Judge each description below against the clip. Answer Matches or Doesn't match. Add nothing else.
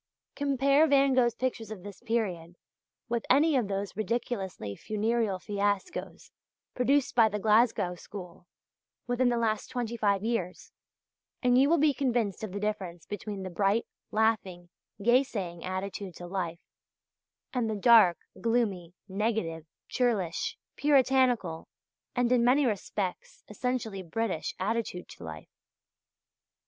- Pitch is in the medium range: Doesn't match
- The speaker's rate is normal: Doesn't match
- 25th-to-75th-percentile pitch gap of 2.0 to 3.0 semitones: Doesn't match